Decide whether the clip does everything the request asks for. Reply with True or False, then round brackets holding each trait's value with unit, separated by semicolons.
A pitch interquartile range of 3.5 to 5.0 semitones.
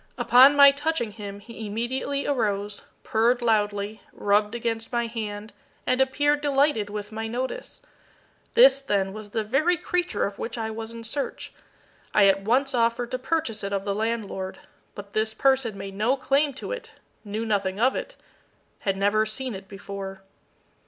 True (4.3 semitones)